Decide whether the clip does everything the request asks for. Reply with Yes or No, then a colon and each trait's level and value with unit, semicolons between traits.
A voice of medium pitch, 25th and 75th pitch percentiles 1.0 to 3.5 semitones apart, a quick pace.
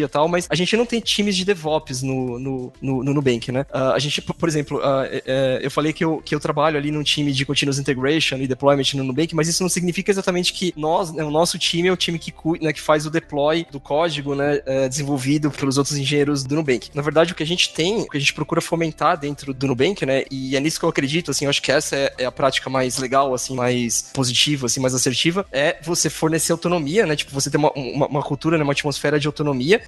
Yes: medium, 145 Hz; average, 3.1 semitones; fast, 245 wpm